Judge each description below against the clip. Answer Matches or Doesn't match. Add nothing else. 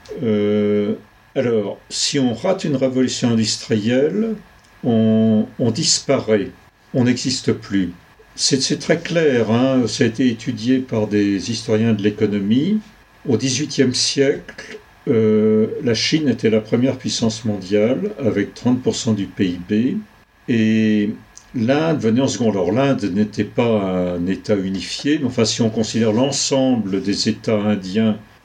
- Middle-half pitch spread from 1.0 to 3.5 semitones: Doesn't match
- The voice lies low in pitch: Matches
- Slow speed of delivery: Matches